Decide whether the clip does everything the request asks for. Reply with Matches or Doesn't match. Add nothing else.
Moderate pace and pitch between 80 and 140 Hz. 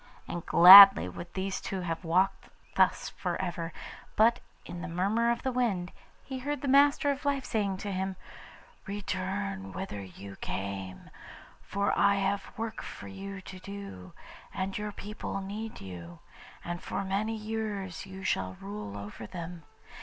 Doesn't match